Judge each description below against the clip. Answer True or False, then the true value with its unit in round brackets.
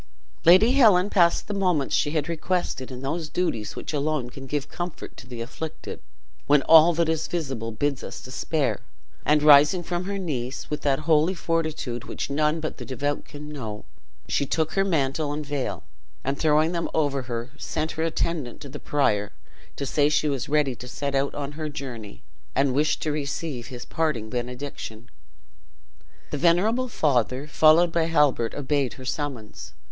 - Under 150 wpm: False (175 wpm)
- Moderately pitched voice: True (145 Hz)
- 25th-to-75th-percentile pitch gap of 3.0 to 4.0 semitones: True (3.5 semitones)